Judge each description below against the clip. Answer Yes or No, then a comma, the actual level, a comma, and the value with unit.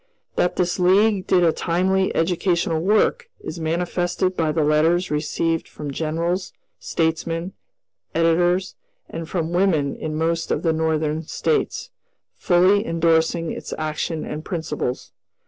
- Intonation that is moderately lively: No, narrow, 2.1 semitones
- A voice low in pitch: No, medium, 165 Hz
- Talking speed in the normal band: No, slow, 130 wpm